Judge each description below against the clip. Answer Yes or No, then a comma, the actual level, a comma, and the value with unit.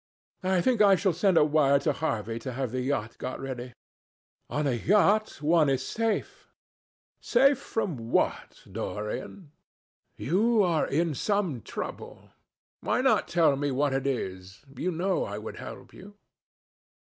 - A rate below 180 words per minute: Yes, average, 150 wpm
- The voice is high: No, medium, 150 Hz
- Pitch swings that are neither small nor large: No, wide, 6.9 semitones